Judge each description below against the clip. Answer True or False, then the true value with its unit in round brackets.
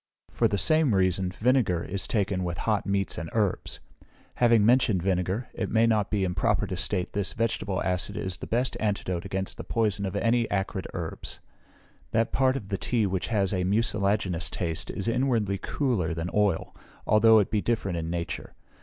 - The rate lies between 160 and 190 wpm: True (180 wpm)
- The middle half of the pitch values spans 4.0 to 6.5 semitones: False (3.6 semitones)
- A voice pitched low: True (100 Hz)